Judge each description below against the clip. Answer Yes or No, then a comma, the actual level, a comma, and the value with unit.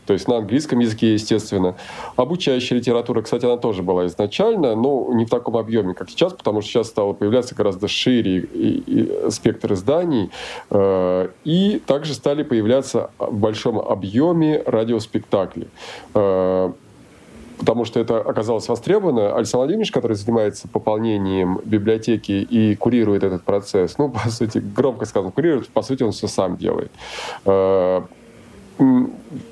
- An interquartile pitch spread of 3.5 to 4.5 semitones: Yes, average, 3.8 semitones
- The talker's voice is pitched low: Yes, low, 110 Hz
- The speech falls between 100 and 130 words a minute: No, average, 140 wpm